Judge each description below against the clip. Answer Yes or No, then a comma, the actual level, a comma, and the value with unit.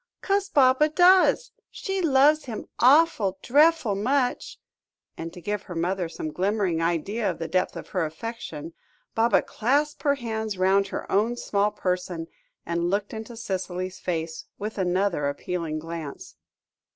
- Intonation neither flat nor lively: No, wide, 5.9 semitones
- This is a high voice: Yes, high, 200 Hz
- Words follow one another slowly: No, average, 145 wpm